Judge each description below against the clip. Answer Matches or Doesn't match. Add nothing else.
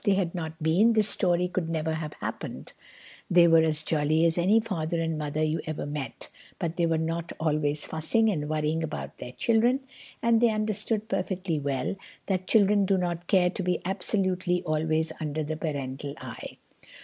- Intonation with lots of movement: Doesn't match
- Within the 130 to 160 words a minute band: Doesn't match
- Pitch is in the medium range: Matches